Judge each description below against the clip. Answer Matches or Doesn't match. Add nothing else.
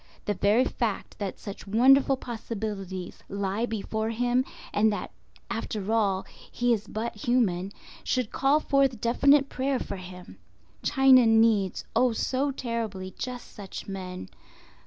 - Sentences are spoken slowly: Matches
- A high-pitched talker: Matches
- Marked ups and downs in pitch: Doesn't match